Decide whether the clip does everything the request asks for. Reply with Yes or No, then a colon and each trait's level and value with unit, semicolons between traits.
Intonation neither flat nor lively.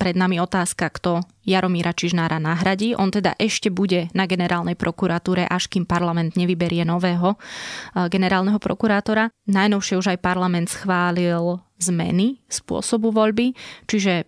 No: narrow, 2.0 semitones